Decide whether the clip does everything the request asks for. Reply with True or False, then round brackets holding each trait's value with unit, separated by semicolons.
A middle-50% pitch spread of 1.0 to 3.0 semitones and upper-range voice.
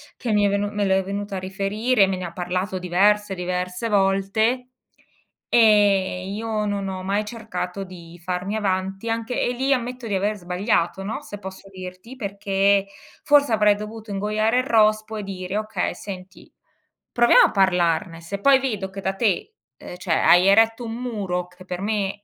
True (2.5 semitones; 200 Hz)